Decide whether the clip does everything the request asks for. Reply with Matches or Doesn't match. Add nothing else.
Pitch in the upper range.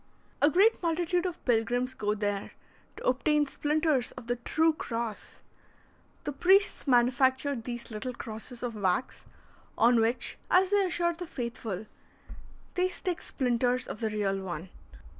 Matches